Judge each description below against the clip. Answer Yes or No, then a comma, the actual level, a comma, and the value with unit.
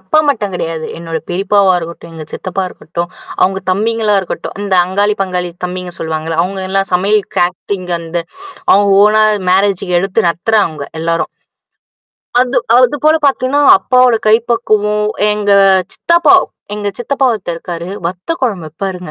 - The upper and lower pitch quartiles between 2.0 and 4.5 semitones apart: Yes, average, 3.6 semitones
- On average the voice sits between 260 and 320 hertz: No, high, 195 Hz